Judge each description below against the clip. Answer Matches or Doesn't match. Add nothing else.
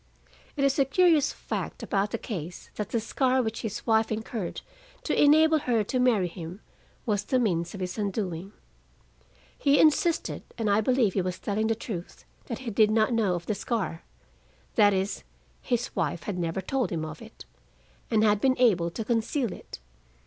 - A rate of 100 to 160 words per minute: Doesn't match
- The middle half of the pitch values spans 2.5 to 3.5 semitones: Doesn't match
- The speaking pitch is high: Matches